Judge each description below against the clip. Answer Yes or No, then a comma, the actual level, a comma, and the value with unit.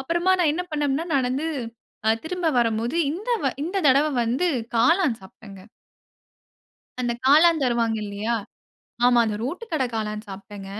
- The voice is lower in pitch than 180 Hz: No, very high, 260 Hz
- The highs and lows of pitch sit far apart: Yes, wide, 6.4 semitones